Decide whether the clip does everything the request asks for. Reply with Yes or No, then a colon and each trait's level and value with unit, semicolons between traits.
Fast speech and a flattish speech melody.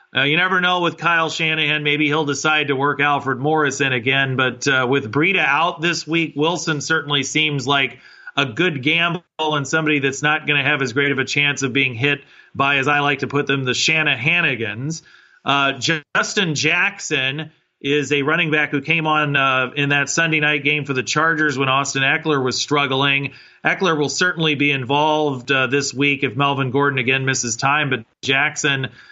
No: average, 195 wpm; narrow, 2.2 semitones